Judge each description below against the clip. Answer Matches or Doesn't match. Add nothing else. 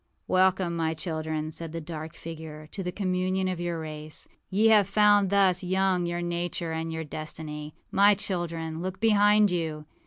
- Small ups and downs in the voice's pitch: Doesn't match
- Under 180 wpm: Matches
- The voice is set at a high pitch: Doesn't match